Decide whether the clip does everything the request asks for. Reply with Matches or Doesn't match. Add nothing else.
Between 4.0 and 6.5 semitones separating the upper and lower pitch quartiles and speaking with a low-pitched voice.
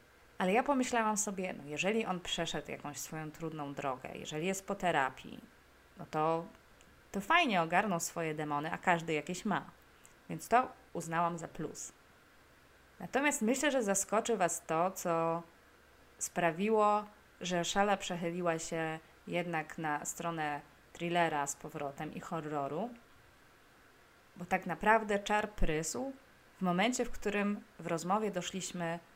Doesn't match